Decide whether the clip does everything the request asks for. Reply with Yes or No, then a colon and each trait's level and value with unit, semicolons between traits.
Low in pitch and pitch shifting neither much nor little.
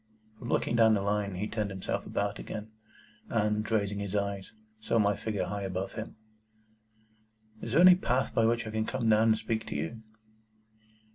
No: low, 105 Hz; narrow, 1.9 semitones